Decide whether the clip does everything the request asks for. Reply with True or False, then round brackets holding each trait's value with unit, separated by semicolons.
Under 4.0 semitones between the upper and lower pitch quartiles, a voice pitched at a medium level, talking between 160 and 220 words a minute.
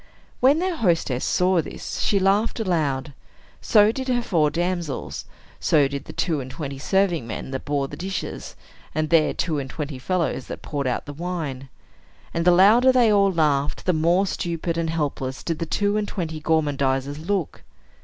False (5.0 semitones; 165 Hz; 180 wpm)